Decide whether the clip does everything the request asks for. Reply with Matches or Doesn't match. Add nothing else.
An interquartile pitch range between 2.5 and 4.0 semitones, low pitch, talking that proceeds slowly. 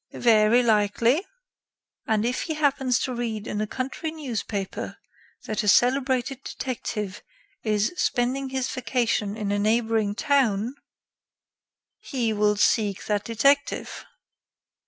Doesn't match